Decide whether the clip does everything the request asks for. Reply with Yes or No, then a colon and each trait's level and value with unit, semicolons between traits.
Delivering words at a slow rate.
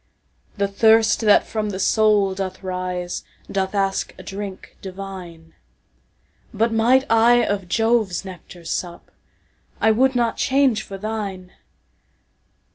Yes: slow, 110 wpm